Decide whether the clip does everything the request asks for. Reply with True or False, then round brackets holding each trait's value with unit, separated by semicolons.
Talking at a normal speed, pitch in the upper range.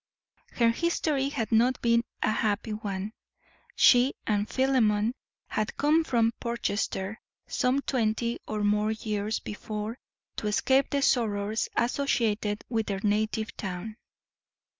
False (120 wpm; 220 Hz)